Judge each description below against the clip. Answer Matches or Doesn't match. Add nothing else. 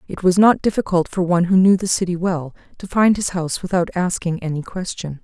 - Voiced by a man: Doesn't match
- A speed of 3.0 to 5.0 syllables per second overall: Doesn't match